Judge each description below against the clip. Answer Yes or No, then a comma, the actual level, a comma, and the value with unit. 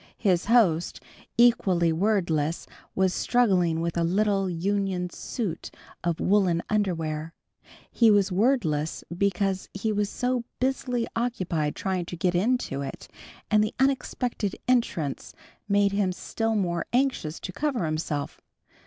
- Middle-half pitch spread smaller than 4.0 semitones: No, average, 4.7 semitones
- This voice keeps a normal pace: No, slow, 125 wpm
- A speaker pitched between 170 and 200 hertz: Yes, high, 190 Hz